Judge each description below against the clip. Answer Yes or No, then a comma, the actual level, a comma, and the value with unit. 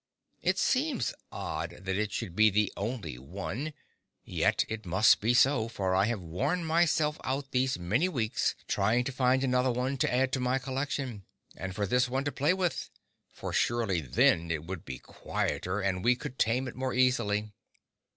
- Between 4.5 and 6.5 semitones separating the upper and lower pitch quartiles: Yes, average, 5.1 semitones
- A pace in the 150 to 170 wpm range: No, average, 180 wpm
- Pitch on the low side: Yes, low, 120 Hz